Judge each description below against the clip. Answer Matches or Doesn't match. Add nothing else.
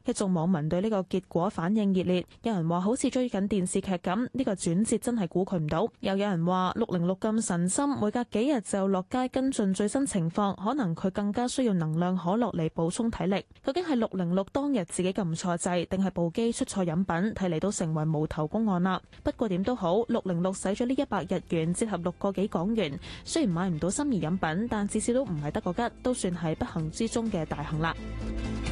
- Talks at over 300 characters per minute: Matches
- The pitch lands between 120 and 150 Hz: Doesn't match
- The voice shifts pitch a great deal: Doesn't match